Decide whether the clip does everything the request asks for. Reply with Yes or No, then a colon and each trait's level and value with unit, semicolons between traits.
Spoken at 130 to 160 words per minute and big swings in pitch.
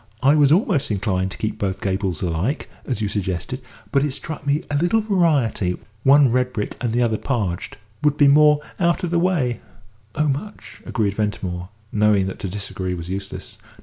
No: average, 185 wpm; wide, 7.2 semitones